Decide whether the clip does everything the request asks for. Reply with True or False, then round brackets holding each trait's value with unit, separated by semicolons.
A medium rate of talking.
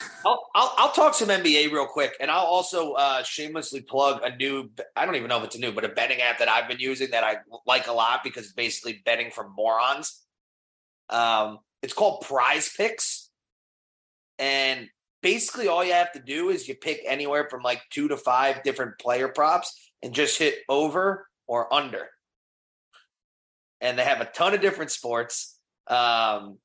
True (180 wpm)